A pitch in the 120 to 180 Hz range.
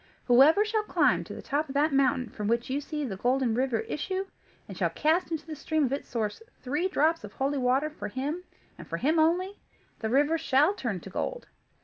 No: very high, 285 Hz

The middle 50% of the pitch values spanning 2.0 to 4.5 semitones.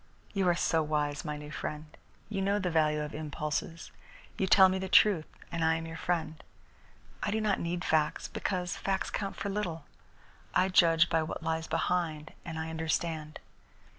Yes: average, 3.0 semitones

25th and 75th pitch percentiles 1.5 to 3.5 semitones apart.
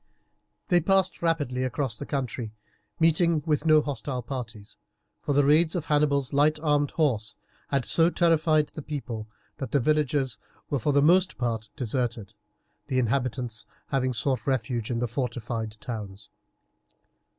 No: average, 4.4 semitones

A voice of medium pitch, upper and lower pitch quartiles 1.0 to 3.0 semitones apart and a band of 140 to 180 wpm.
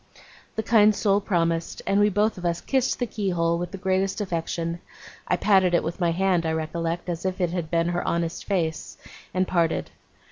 No: medium, 175 Hz; narrow, 2.6 semitones; average, 200 wpm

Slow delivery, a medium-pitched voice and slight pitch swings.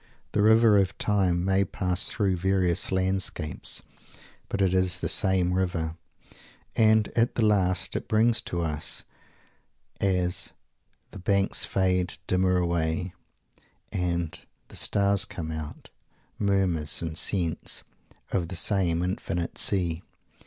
No: slow, 125 wpm; very low, 95 Hz; narrow, 2.3 semitones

